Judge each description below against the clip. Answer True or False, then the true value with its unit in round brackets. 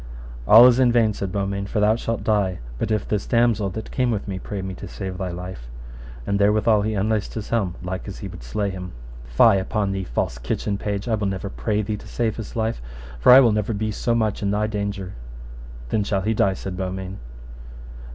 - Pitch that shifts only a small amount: True (2.3 semitones)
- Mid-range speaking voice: False (100 Hz)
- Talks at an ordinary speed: False (220 wpm)